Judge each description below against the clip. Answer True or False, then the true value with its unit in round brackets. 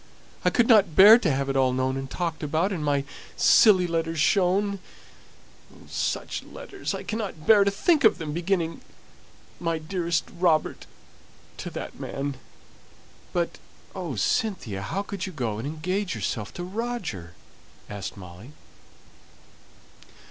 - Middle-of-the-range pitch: True (165 Hz)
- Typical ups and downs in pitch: False (6.2 semitones)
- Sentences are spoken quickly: False (140 wpm)